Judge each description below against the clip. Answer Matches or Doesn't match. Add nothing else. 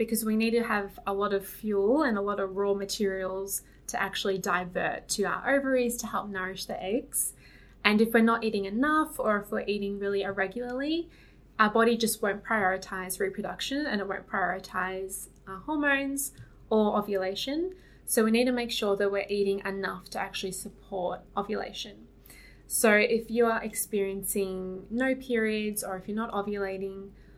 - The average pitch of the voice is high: Matches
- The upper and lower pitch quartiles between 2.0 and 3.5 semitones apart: Matches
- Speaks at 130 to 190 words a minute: Matches